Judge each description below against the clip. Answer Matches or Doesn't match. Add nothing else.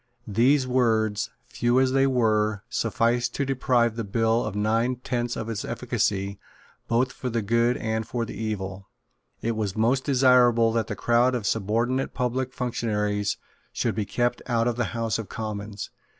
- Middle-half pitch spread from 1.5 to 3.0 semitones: Matches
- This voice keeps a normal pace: Matches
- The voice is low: Matches